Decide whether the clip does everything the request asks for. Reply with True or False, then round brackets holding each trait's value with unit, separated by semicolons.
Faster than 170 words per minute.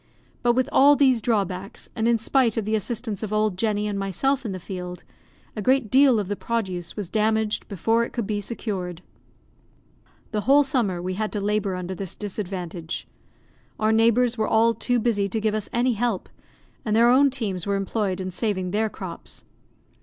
True (190 wpm)